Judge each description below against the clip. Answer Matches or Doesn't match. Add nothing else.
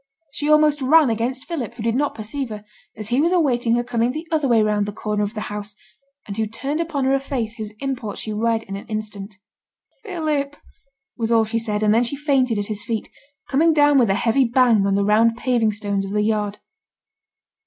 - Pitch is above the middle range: Matches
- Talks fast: Matches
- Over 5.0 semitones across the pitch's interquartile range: Doesn't match